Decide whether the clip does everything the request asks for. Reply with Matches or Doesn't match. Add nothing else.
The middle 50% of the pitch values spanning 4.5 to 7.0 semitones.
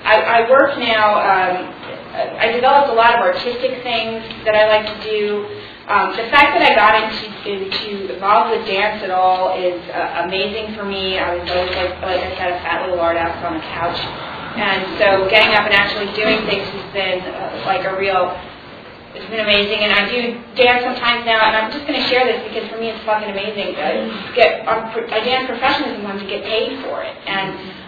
Doesn't match